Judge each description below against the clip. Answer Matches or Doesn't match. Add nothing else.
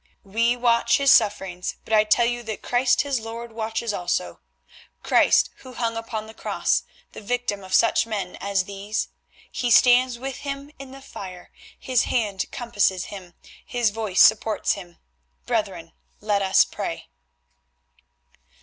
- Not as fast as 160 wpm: Matches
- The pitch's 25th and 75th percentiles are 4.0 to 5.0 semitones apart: Doesn't match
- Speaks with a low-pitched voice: Doesn't match